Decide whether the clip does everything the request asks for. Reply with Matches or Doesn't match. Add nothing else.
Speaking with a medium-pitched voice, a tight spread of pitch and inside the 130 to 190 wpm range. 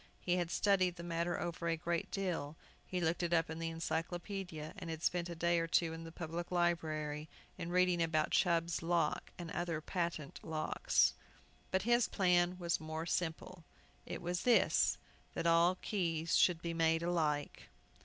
Matches